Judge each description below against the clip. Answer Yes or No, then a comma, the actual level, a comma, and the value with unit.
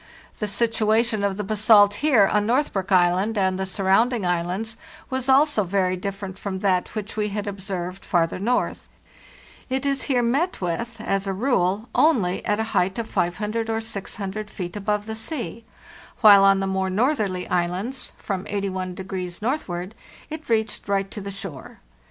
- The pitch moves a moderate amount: Yes, average, 3.0 semitones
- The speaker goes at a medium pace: Yes, average, 165 wpm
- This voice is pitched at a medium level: No, high, 205 Hz